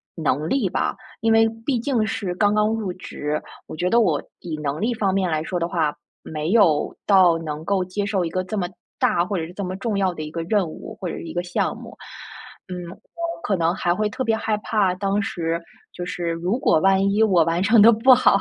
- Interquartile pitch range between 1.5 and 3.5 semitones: No, average, 4.0 semitones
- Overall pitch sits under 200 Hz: Yes, medium, 185 Hz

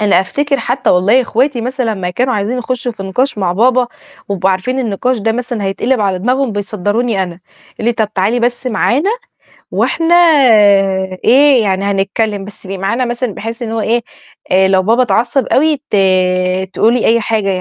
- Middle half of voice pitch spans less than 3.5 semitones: No, average, 4.2 semitones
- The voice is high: Yes, high, 225 Hz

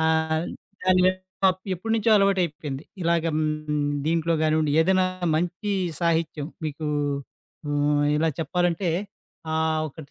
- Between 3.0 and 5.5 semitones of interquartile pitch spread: No, narrow, 2.6 semitones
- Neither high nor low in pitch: Yes, medium, 160 Hz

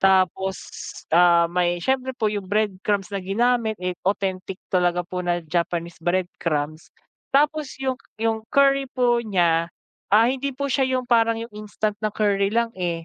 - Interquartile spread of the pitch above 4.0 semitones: Yes, average, 5.0 semitones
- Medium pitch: No, high, 200 Hz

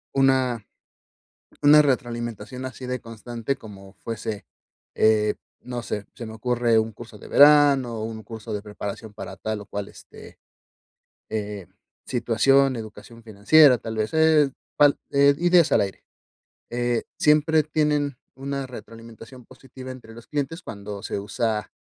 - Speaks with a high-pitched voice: No, low, 120 Hz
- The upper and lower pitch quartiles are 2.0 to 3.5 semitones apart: No, average, 4.0 semitones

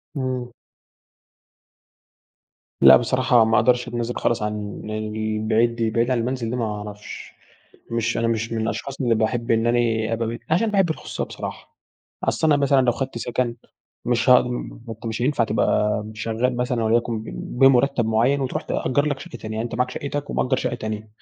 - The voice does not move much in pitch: Yes, narrow, 2.3 semitones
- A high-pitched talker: No, low, 115 Hz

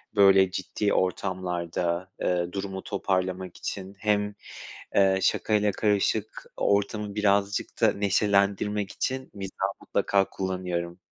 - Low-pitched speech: Yes, low, 100 Hz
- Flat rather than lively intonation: Yes, narrow, 1.6 semitones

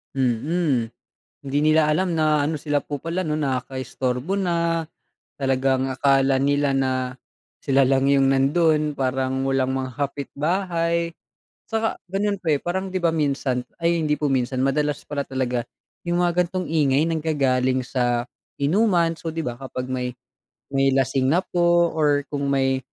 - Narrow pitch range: No, average, 3.8 semitones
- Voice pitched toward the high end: No, medium, 145 Hz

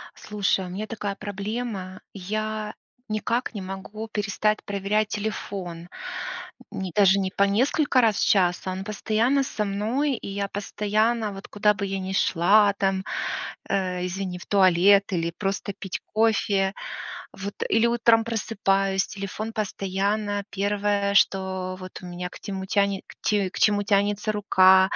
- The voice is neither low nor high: No, high, 200 Hz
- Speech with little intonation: Yes, narrow, 1.9 semitones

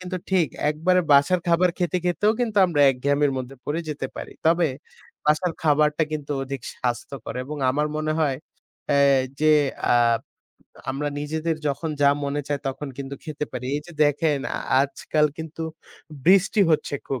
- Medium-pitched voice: Yes, medium, 150 Hz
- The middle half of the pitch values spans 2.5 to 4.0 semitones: Yes, average, 2.8 semitones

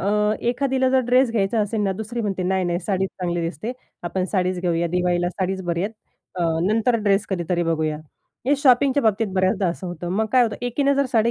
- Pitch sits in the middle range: No, high, 195 Hz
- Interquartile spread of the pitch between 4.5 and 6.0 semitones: Yes, average, 4.9 semitones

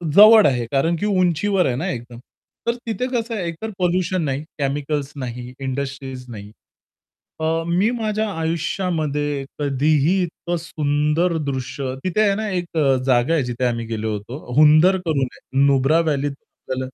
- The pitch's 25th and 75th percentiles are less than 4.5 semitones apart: No, average, 5.2 semitones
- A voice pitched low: No, medium, 150 Hz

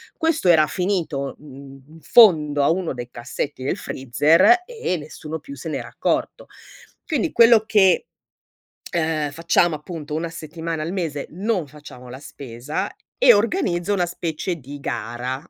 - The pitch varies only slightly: No, average, 4.7 semitones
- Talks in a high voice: No, medium, 160 Hz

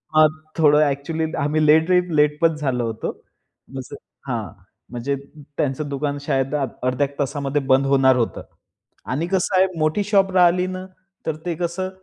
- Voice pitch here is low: No, medium, 150 Hz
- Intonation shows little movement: No, average, 3.6 semitones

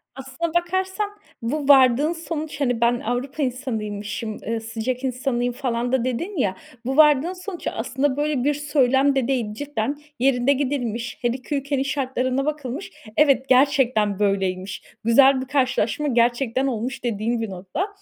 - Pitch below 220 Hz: No, very high, 260 Hz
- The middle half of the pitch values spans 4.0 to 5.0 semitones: No, average, 3.3 semitones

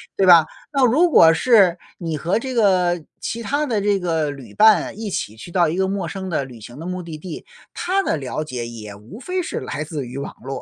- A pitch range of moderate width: No, wide, 6.2 semitones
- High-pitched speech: No, medium, 175 Hz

